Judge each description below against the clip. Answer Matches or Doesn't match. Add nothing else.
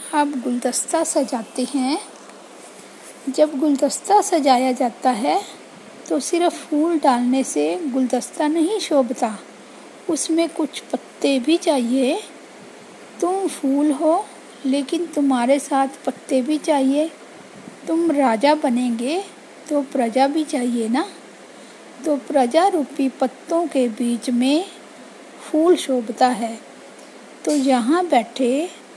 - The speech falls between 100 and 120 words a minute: Matches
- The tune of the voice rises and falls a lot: Doesn't match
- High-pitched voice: Matches